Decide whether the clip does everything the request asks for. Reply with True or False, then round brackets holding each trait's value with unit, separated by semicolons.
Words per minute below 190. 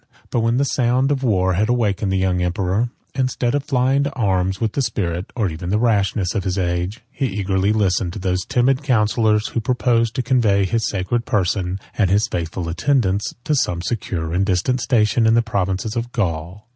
False (195 wpm)